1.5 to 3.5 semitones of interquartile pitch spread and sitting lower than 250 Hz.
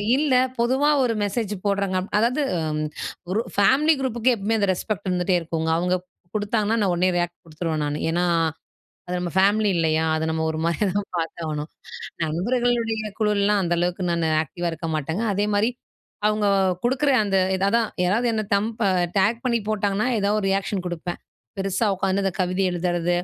No: average, 3.9 semitones; high, 195 Hz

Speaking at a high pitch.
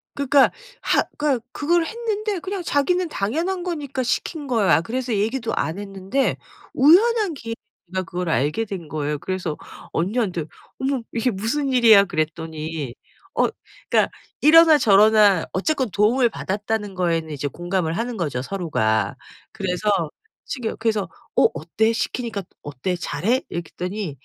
Yes: high, 215 Hz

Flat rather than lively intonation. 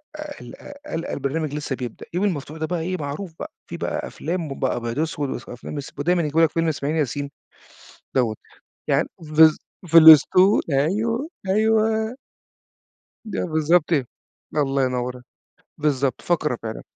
No: average, 4.3 semitones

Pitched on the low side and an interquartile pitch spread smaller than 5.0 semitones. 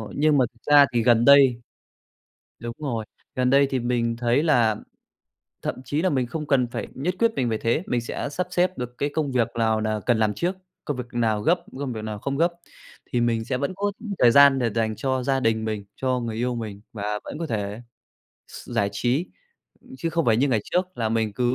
Yes: low, 125 Hz; average, 3.9 semitones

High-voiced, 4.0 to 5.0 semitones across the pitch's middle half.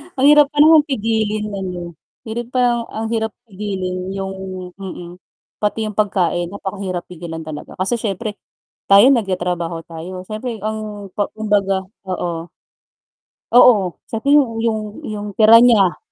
No: high, 205 Hz; average, 3.4 semitones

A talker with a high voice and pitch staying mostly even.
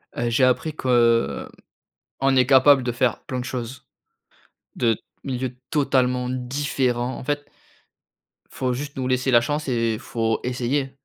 No: low, 125 Hz; narrow, 1.8 semitones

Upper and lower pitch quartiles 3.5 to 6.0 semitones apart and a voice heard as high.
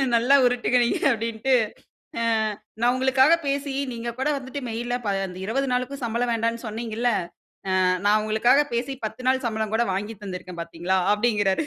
No: average, 3.1 semitones; high, 235 Hz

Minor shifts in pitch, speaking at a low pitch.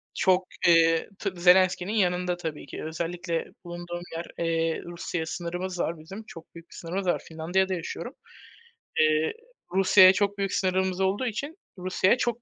No: narrow, 2.2 semitones; medium, 180 Hz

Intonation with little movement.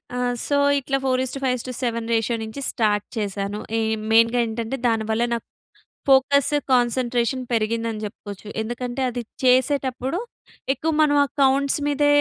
No: average, 3.0 semitones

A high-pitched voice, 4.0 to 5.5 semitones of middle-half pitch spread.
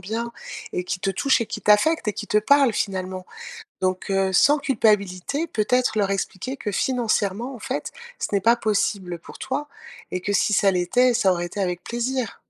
Yes: high, 210 Hz; average, 4.6 semitones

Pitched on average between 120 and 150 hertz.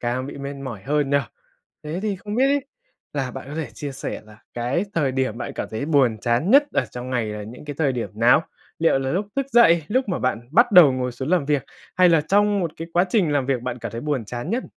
Yes: medium, 140 Hz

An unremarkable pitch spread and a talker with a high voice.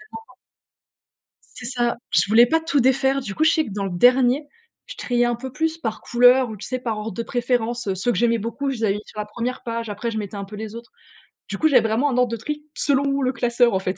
Yes: average, 3.0 semitones; high, 240 Hz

